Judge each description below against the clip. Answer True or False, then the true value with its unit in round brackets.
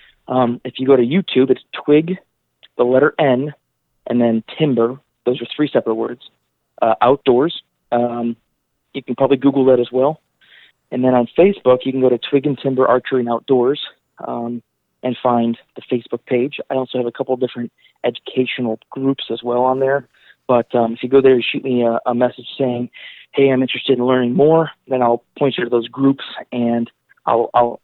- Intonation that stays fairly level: True (2.1 semitones)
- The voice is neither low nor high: False (125 Hz)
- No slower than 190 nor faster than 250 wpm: True (195 wpm)